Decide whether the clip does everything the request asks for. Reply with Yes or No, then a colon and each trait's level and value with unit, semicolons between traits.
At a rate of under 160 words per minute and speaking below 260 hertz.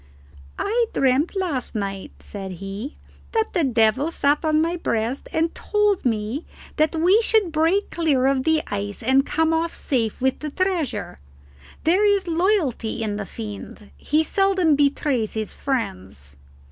No: average, 150 wpm; very high, 285 Hz